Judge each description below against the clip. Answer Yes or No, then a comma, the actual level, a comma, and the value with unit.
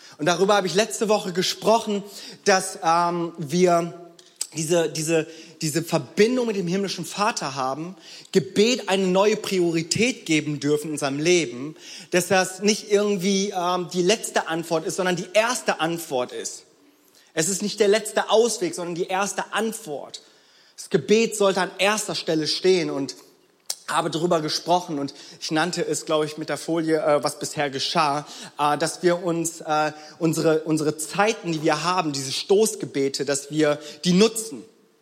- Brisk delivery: No, average, 155 wpm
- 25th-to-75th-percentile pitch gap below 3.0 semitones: No, average, 4.1 semitones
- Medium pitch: Yes, medium, 175 Hz